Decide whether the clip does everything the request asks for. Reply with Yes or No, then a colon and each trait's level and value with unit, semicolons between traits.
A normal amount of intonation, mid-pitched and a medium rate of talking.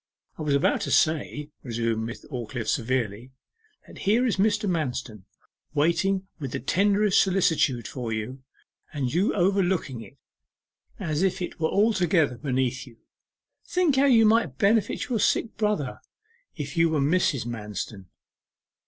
No: wide, 7.8 semitones; medium, 155 Hz; average, 145 wpm